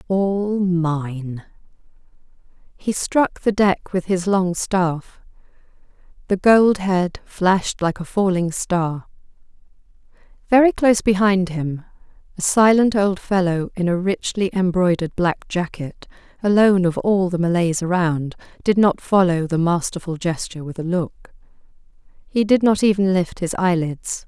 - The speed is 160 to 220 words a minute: No, slow, 135 wpm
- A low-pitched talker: No, medium, 185 Hz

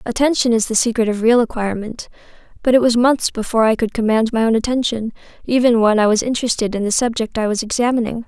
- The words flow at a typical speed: No, fast, 210 wpm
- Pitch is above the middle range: Yes, high, 230 Hz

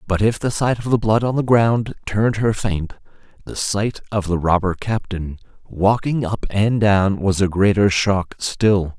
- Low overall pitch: Yes, low, 100 Hz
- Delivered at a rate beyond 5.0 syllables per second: No, 4.3 syllables/s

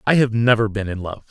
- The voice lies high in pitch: No, low, 110 Hz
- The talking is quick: Yes, fast, 275 wpm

